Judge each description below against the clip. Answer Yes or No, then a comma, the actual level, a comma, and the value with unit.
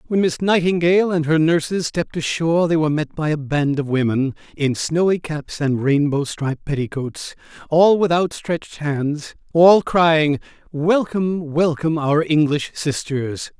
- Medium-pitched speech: Yes, medium, 155 Hz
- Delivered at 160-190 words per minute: No, average, 150 wpm